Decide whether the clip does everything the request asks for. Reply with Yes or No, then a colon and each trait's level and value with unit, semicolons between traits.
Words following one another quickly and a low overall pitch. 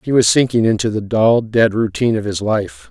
Yes: fast, 225 wpm; low, 110 Hz